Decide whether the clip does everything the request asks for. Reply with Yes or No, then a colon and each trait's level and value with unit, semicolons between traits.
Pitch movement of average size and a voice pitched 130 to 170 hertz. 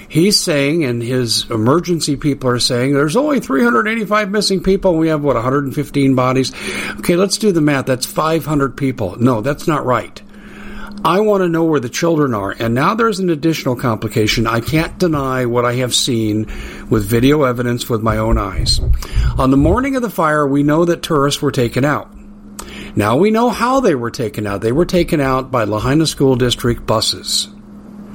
No: wide, 6.3 semitones; medium, 140 Hz